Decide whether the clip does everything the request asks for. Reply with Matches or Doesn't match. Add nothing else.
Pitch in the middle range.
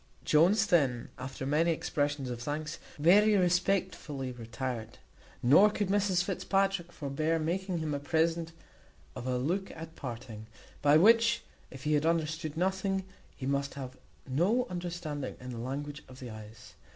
Matches